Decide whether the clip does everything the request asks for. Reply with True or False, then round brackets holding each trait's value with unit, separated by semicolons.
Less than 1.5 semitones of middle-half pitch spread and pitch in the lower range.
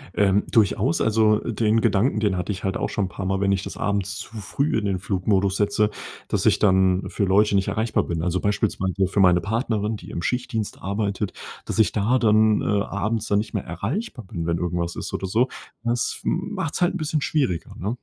False (2.7 semitones; 100 Hz)